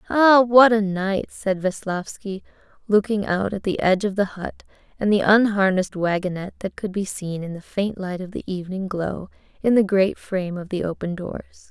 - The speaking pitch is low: No, high, 195 Hz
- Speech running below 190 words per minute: No, average, 195 wpm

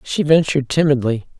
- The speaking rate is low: Yes, slow, 130 wpm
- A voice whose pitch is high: No, medium, 150 Hz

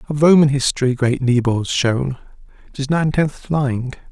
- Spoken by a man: Yes, male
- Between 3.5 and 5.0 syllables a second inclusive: Yes, 4.7 syllables/s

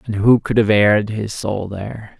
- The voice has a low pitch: Yes, low, 105 Hz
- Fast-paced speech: Yes, fast, 220 wpm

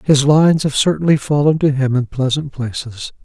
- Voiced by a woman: No, male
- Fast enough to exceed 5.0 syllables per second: Yes, 5.2 syllables/s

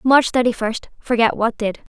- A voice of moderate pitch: No, high, 235 Hz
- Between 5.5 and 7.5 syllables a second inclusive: No, 4.9 syllables/s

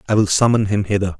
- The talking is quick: Yes, fast, 250 wpm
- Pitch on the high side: No, low, 100 Hz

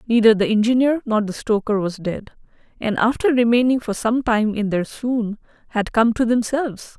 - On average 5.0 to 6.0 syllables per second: Yes, 5.1 syllables/s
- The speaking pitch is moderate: No, high, 225 Hz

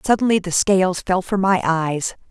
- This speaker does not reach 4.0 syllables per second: No, 4.8 syllables/s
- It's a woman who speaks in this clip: Yes, female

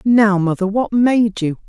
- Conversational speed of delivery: Yes, average, 180 wpm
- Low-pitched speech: No, high, 210 Hz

